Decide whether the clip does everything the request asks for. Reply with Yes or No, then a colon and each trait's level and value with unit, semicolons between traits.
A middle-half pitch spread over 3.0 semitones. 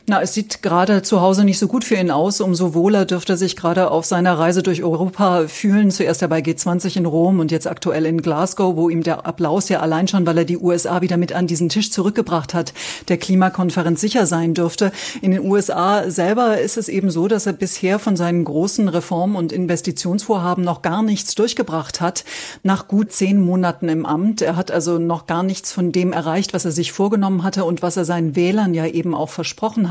No: narrow, 2.5 semitones